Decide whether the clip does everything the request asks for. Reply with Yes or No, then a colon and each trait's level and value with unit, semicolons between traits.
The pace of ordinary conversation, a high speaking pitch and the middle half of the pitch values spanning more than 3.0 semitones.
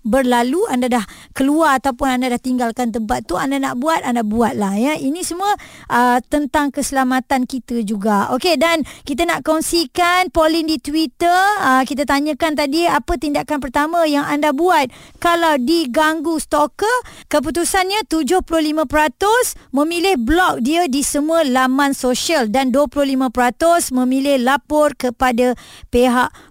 Yes: average, 135 wpm; very high, 290 Hz; average, 4.1 semitones